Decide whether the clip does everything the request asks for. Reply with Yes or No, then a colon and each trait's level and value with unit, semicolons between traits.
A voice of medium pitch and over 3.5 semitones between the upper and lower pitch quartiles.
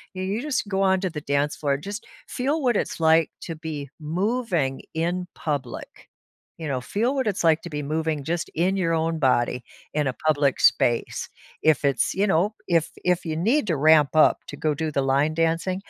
Yes: medium, 160 Hz; average, 4.2 semitones